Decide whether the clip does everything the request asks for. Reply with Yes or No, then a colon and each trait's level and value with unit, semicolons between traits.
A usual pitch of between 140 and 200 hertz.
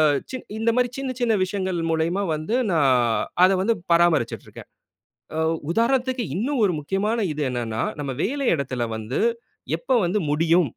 Yes: medium, 185 Hz